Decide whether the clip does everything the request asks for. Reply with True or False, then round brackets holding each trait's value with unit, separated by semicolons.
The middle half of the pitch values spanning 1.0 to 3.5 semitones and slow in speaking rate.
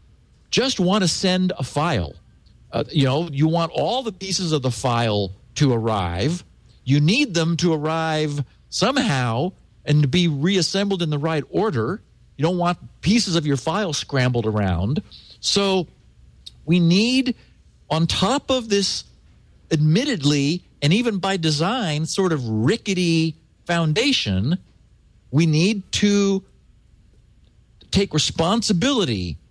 False (5.6 semitones; 130 wpm)